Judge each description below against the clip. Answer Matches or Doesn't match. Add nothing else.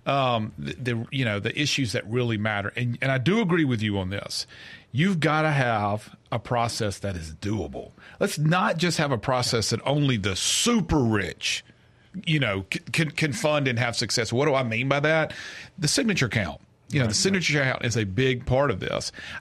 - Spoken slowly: Doesn't match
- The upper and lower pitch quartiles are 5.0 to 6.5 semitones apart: Matches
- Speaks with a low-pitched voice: Matches